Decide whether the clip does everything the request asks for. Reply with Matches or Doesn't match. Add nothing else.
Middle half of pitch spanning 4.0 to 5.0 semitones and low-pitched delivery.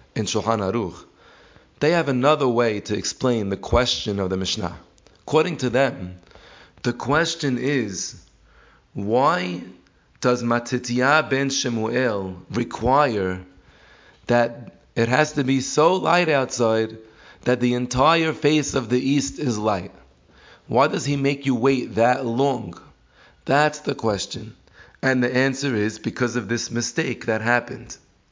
Matches